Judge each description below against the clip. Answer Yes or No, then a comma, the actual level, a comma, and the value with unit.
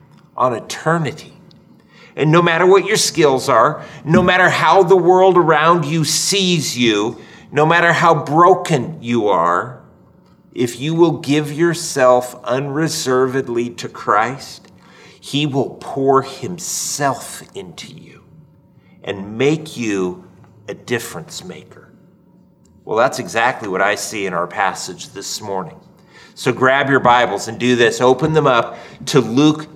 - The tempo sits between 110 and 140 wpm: Yes, slow, 135 wpm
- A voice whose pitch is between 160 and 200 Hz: No, medium, 150 Hz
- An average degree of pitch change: Yes, average, 5.0 semitones